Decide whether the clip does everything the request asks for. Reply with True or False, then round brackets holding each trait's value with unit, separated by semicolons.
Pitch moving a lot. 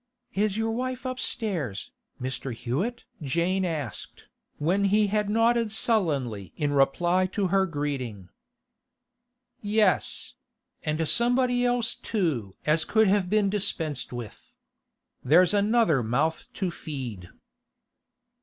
True (7.2 semitones)